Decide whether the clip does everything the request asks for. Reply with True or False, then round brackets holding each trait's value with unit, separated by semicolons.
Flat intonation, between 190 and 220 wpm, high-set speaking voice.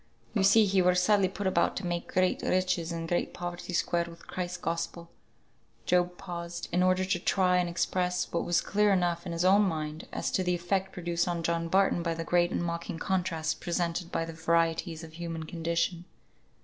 False (1.5 semitones; 200 wpm; 175 Hz)